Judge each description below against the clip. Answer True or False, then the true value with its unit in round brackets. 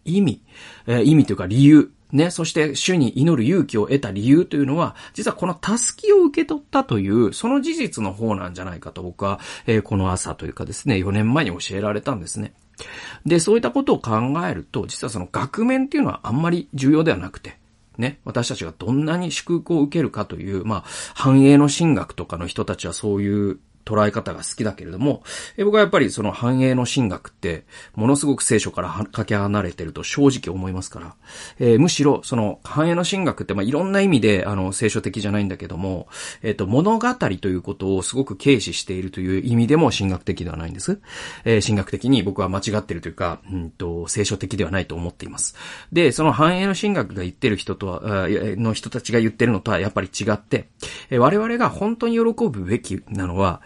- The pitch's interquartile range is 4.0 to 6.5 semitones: False (7.2 semitones)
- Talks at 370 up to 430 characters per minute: True (405 characters per minute)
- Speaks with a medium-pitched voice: False (110 Hz)